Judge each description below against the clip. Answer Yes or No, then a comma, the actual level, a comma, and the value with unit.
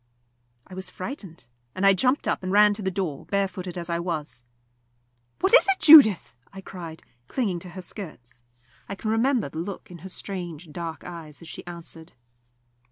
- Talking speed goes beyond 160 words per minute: Yes, average, 180 wpm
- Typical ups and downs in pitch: Yes, average, 3.1 semitones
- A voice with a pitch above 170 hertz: Yes, medium, 185 Hz